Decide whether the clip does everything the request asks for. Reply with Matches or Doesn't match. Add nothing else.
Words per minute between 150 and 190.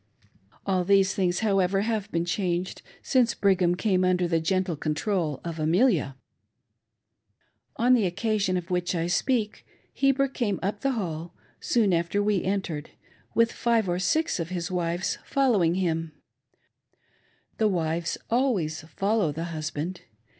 Doesn't match